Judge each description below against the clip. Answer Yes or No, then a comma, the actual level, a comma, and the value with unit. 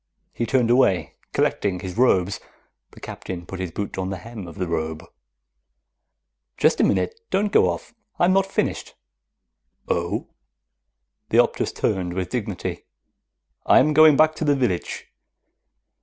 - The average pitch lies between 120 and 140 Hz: No, low, 100 Hz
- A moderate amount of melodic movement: No, wide, 7.9 semitones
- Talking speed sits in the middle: Yes, average, 145 wpm